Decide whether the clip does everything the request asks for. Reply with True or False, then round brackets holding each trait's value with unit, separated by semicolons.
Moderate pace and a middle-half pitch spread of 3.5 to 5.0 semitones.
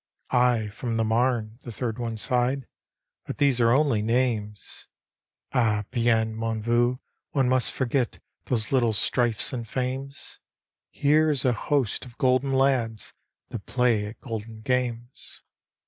False (145 wpm; 2.4 semitones)